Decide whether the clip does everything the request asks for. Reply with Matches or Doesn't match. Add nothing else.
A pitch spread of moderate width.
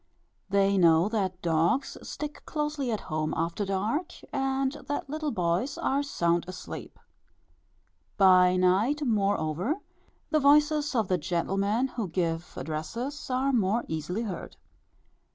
Doesn't match